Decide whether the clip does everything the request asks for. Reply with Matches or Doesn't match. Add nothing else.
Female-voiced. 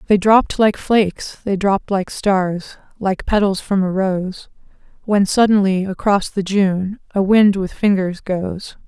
Matches